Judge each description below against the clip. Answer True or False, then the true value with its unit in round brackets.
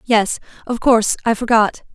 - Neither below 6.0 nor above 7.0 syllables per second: False (5.0 syllables/s)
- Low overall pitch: False (225 Hz)